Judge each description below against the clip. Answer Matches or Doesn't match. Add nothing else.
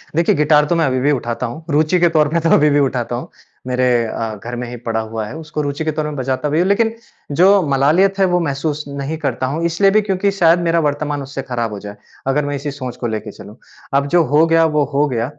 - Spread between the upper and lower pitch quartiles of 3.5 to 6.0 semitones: Matches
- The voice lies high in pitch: Doesn't match